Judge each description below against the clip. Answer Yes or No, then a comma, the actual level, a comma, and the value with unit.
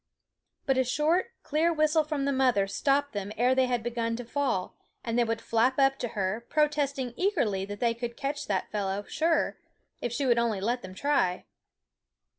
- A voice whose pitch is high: Yes, high, 245 Hz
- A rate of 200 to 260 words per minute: No, average, 190 wpm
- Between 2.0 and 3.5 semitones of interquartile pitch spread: No, average, 4.2 semitones